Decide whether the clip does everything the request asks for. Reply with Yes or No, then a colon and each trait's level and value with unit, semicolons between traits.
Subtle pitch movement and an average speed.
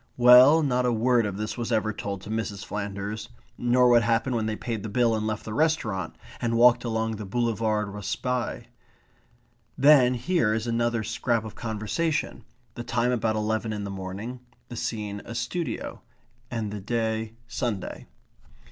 Yes: narrow, 2.3 semitones; average, 165 wpm